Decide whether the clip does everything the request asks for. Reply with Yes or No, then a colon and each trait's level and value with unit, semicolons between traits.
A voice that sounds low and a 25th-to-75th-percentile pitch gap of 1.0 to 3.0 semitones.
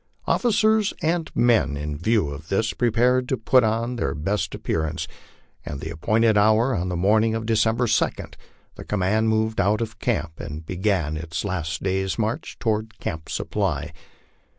No: low, 110 Hz; wide, 5.4 semitones